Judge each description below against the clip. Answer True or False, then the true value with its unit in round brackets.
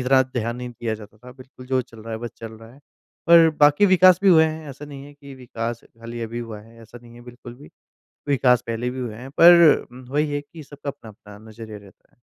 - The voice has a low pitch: True (125 Hz)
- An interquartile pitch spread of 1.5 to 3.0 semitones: False (3.9 semitones)